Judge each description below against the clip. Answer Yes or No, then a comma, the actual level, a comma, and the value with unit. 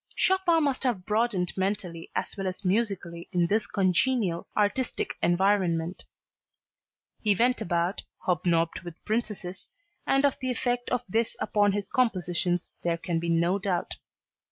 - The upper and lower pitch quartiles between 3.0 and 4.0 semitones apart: No, average, 4.9 semitones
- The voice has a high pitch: Yes, high, 195 Hz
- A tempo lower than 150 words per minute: Yes, average, 140 wpm